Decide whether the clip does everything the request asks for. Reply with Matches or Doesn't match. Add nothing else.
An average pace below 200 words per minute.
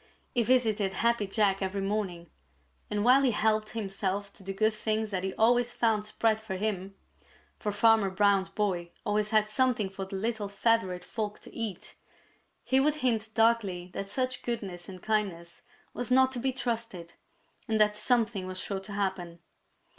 Matches